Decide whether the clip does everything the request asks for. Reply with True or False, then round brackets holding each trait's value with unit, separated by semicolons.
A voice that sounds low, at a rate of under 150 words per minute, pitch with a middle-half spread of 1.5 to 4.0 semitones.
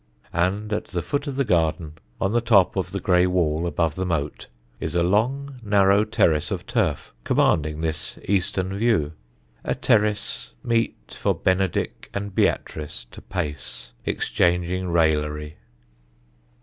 False (90 Hz; 140 wpm; 4.5 semitones)